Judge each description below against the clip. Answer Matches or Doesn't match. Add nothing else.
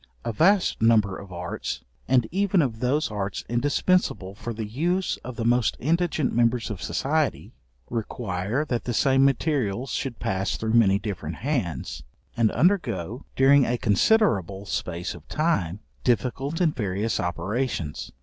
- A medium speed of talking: Matches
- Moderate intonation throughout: Doesn't match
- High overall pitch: Doesn't match